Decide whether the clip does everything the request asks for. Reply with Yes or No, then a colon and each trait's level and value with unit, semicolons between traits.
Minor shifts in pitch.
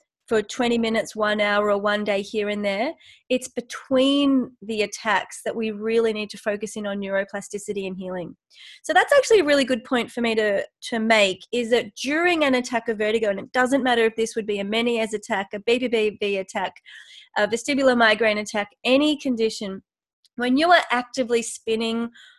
No: average, 3.4 semitones